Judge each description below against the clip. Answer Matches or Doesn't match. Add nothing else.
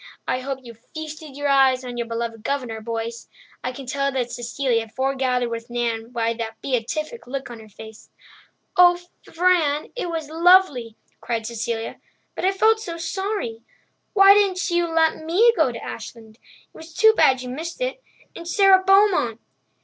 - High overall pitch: Matches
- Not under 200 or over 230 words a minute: Doesn't match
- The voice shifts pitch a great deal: Matches